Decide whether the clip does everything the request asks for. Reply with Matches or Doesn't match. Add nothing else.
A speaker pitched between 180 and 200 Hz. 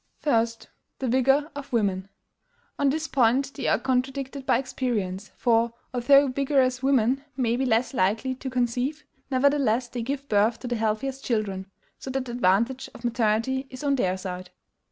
Doesn't match